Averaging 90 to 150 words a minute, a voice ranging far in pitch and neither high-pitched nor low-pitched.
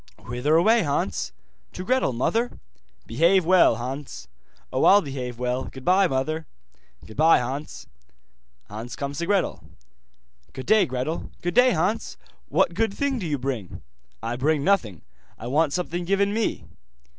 Yes: average, 145 wpm; wide, 7.0 semitones; medium, 155 Hz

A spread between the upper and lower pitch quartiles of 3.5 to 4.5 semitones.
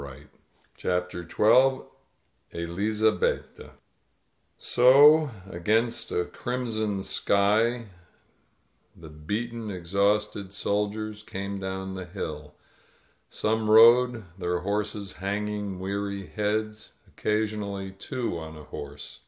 No: narrow, 2.6 semitones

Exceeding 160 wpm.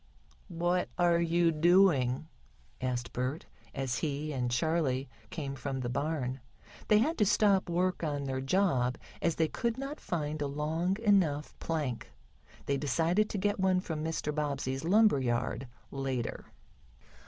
No: average, 145 wpm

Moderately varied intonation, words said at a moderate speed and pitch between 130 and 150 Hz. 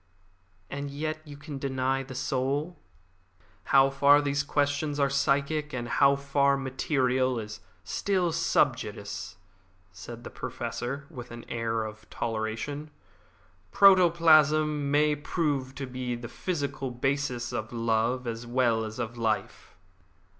No: average, 3.4 semitones; slow, 130 wpm; low, 135 Hz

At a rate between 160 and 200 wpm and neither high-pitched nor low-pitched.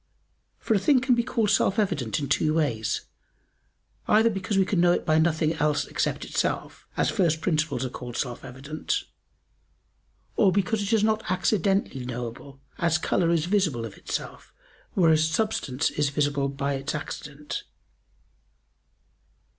No: average, 150 wpm; medium, 160 Hz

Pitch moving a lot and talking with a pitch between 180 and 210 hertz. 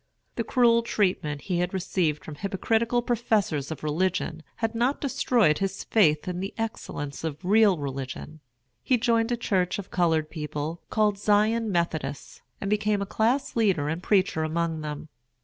Yes: wide, 5.9 semitones; high, 190 Hz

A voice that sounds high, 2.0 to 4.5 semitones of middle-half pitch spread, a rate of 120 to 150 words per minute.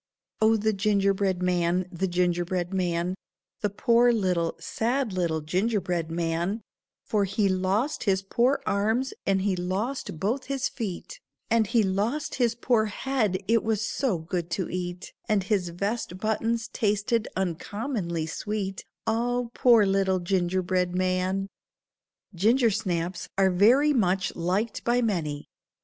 Yes: high, 195 Hz; average, 3.8 semitones; average, 140 wpm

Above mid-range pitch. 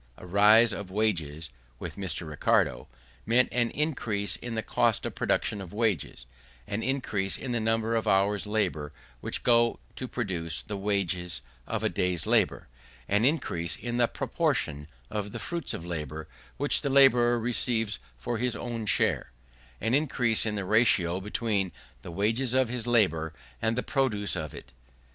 No: low, 105 Hz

